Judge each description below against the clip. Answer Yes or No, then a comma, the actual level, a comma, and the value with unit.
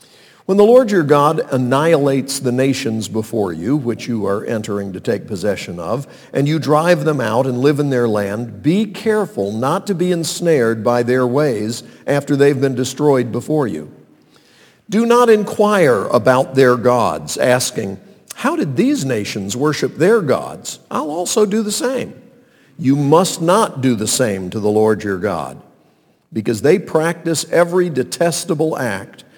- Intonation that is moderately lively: No, wide, 6.1 semitones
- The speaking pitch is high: No, medium, 140 Hz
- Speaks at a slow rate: No, average, 160 wpm